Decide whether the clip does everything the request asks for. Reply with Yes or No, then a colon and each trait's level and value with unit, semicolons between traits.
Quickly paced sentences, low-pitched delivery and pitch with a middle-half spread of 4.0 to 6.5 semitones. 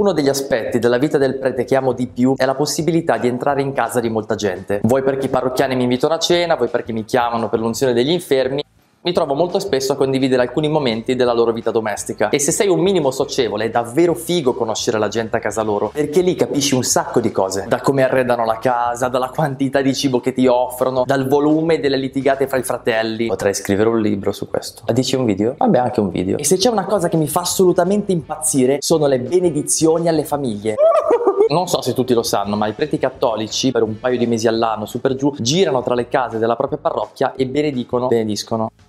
Yes: fast, 230 wpm; low, 130 Hz; average, 4.3 semitones